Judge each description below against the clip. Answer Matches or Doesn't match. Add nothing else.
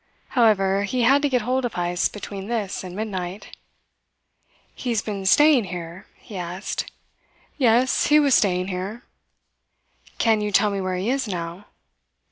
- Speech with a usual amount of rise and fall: Matches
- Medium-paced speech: Matches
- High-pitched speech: Matches